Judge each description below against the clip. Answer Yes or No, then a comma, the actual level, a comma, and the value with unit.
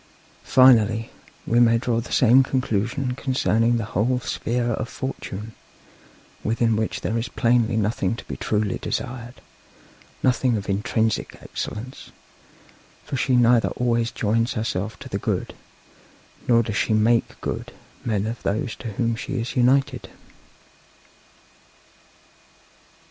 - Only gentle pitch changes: Yes, narrow, 2.1 semitones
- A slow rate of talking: Yes, slow, 125 wpm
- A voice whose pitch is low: Yes, low, 115 Hz